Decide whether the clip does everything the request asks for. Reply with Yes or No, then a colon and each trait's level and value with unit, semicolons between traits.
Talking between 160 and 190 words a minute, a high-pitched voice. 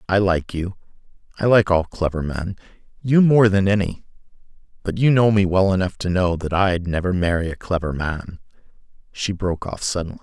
No: average, 170 wpm; very low, 95 Hz